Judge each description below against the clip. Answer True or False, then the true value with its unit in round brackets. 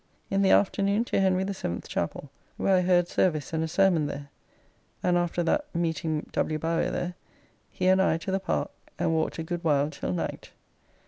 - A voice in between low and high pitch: True (175 Hz)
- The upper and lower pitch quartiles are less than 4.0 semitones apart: True (3.2 semitones)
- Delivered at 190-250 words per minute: True (195 wpm)